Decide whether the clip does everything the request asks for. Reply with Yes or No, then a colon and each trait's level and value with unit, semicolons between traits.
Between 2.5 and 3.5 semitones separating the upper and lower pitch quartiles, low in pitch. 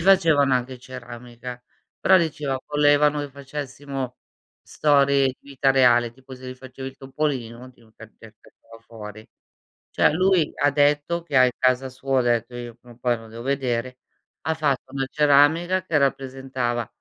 Yes: average, 2.9 semitones; low, 130 Hz